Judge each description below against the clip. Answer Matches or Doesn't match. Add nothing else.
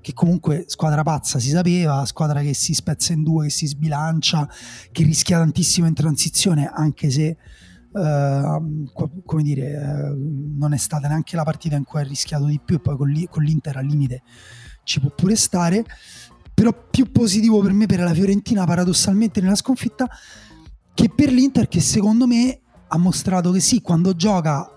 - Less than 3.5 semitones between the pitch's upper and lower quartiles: Doesn't match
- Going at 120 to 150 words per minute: Doesn't match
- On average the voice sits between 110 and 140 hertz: Doesn't match